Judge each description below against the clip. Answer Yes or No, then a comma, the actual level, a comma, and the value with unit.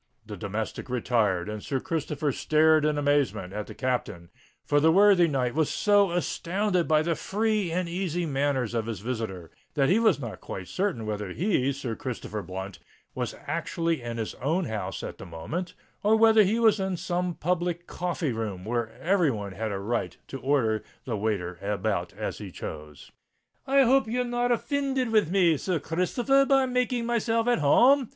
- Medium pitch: Yes, medium, 155 Hz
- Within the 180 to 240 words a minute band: Yes, average, 185 wpm